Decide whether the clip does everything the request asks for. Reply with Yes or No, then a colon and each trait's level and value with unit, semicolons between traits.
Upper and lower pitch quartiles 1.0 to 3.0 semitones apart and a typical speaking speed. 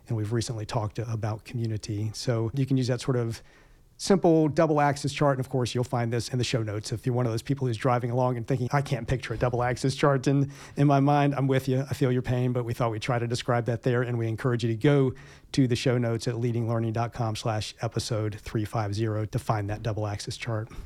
No: average, 2.7 semitones; fast, 245 wpm